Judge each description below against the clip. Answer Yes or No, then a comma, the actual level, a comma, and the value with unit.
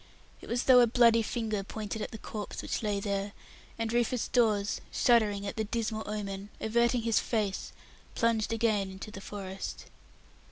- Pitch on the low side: No, high, 220 Hz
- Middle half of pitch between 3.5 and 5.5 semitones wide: No, narrow, 2.4 semitones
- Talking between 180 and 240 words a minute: No, average, 170 wpm